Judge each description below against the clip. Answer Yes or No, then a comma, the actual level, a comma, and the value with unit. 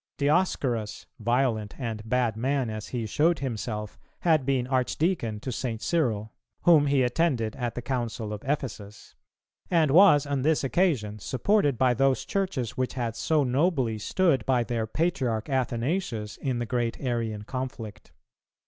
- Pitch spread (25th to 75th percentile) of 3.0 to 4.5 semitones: Yes, average, 4.2 semitones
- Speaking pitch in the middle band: No, low, 125 Hz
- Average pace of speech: Yes, average, 150 wpm